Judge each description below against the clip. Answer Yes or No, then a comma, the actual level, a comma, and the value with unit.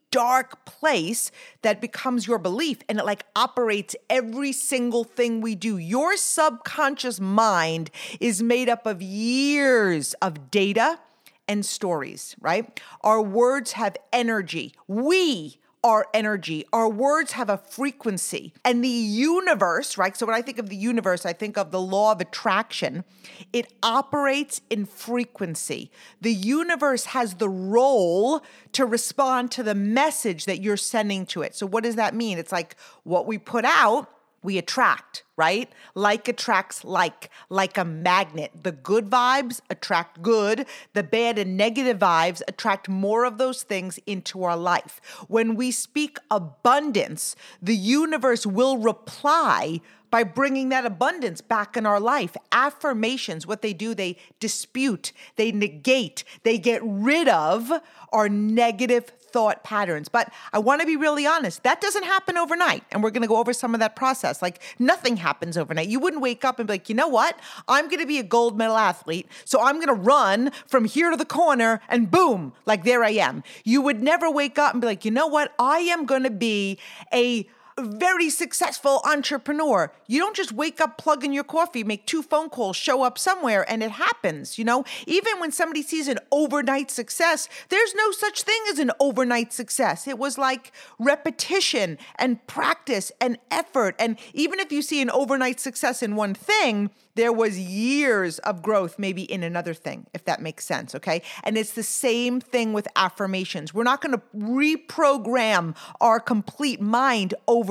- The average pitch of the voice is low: No, high, 235 Hz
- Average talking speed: Yes, average, 175 wpm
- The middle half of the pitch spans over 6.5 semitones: No, average, 5.1 semitones